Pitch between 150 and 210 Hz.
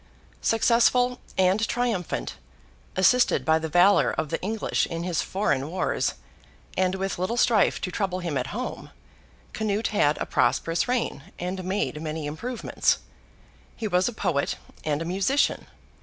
Yes: medium, 185 Hz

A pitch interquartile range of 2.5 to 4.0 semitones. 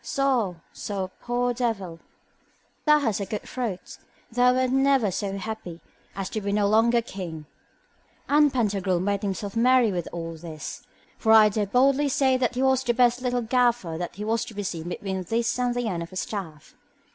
No: average, 4.5 semitones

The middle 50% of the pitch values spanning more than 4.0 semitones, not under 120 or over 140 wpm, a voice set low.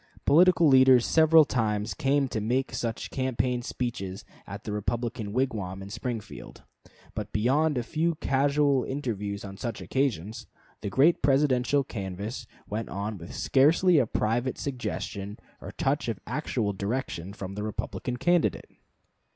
Yes: average, 4.7 semitones; slow, 135 wpm; low, 120 Hz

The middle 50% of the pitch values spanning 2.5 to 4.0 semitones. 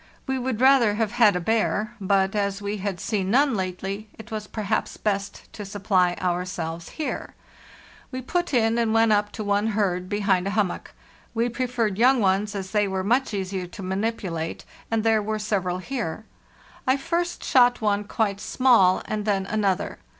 Yes: average, 2.9 semitones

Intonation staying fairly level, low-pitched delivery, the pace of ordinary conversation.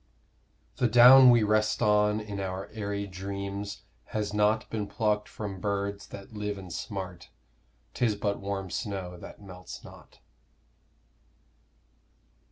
No: narrow, 1.4 semitones; low, 100 Hz; slow, 125 wpm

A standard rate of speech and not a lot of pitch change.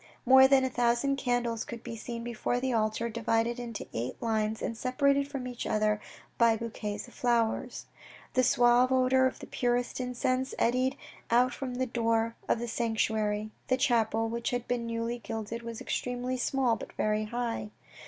Yes: average, 175 wpm; narrow, 1.9 semitones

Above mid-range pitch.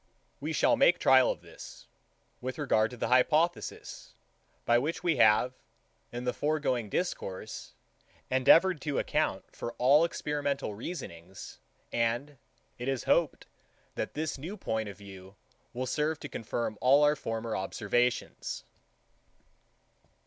No: low, 130 Hz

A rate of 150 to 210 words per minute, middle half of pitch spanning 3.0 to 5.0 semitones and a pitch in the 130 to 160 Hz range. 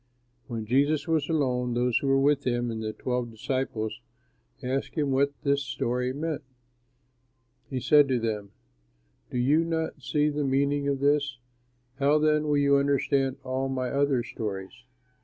No: average, 160 wpm; narrow, 2.5 semitones; low, 135 Hz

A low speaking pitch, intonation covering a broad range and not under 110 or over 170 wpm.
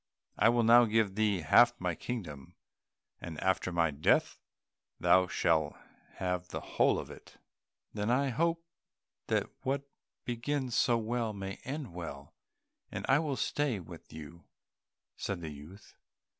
Yes: low, 105 Hz; wide, 6.2 semitones; average, 145 wpm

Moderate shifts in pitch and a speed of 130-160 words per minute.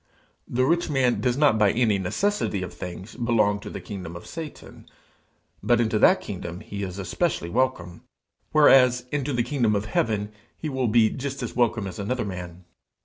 No: average, 4.6 semitones; average, 180 wpm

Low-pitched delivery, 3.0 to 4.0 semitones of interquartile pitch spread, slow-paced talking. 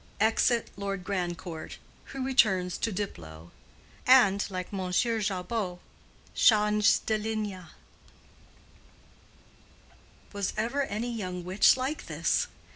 No: high, 205 Hz; average, 3.6 semitones; slow, 100 wpm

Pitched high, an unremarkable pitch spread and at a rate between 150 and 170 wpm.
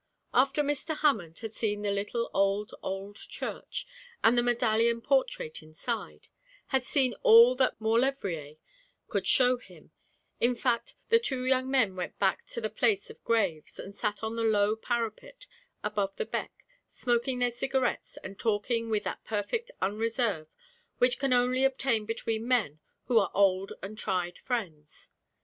Yes: high, 230 Hz; average, 3.7 semitones; average, 155 wpm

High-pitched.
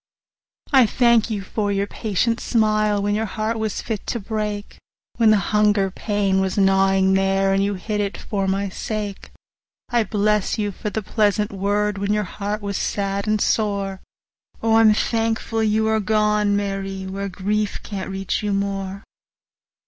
Yes: high, 205 Hz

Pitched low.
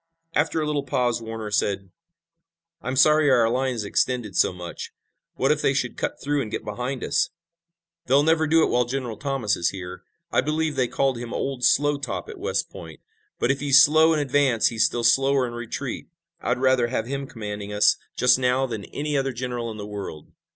Yes: low, 125 Hz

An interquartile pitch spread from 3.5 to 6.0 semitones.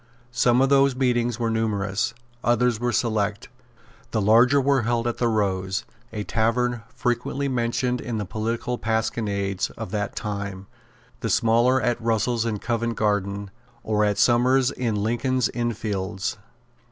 No: average, 2.7 semitones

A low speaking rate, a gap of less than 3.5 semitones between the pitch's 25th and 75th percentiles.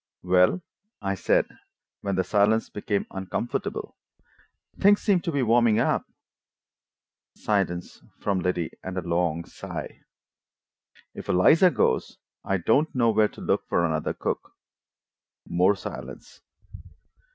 No: slow, 120 wpm; average, 4.3 semitones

